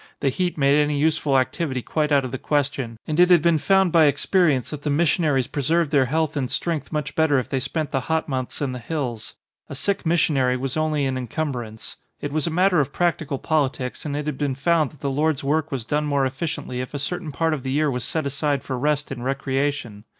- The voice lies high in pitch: No, medium, 145 Hz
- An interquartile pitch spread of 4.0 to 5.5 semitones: No, average, 3.0 semitones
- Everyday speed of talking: No, fast, 235 wpm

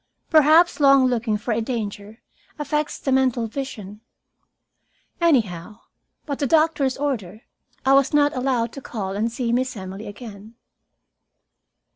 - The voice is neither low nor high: No, high, 245 Hz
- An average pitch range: Yes, average, 4.4 semitones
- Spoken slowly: Yes, slow, 130 wpm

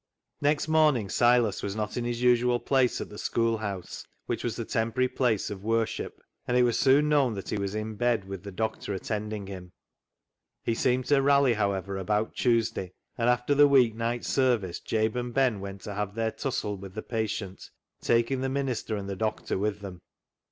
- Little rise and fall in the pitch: No, average, 3.4 semitones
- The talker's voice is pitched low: Yes, low, 115 Hz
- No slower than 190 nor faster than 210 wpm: Yes, average, 195 wpm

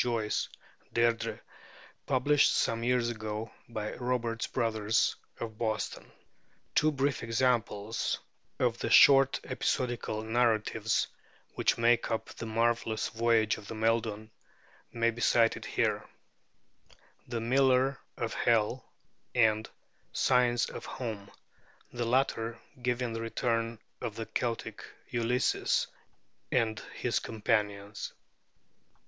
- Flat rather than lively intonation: Yes, narrow, 1.7 semitones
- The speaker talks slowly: Yes, slow, 105 wpm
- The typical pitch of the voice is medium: No, low, 115 Hz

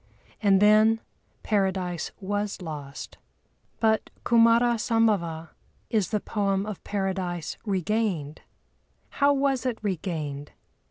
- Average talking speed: No, slow, 100 wpm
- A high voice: Yes, high, 200 Hz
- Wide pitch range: No, average, 4.0 semitones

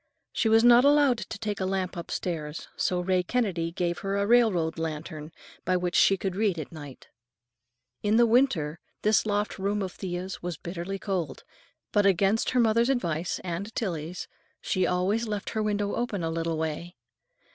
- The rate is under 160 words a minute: No, average, 165 wpm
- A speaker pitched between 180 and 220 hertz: Yes, high, 190 Hz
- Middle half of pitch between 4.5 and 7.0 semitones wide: No, average, 3.9 semitones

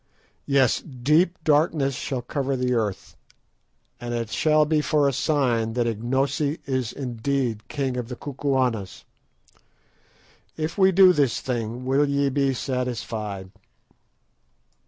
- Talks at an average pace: No, slow, 125 wpm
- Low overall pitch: Yes, low, 130 Hz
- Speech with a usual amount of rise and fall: Yes, average, 3.3 semitones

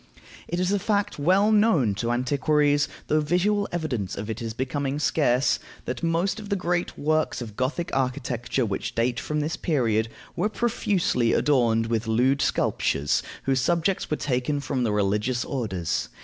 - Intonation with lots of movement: Yes, wide, 6.1 semitones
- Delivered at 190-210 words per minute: No, average, 165 wpm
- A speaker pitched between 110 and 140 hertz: Yes, low, 135 Hz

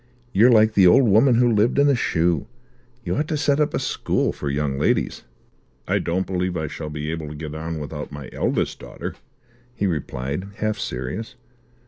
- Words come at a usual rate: Yes, average, 190 wpm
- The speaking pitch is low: Yes, very low, 90 Hz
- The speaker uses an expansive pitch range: Yes, wide, 6.9 semitones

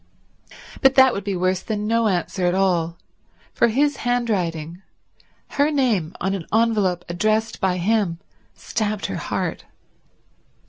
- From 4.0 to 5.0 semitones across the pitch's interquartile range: Yes, average, 4.4 semitones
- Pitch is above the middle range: Yes, high, 205 Hz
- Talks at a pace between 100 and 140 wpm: Yes, slow, 135 wpm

